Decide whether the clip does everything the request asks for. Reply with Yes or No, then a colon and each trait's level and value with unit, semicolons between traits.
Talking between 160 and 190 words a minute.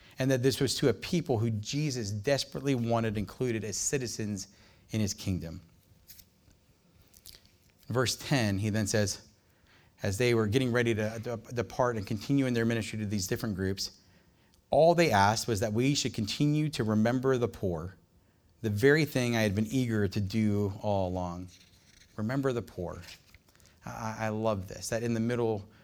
Yes: average, 165 wpm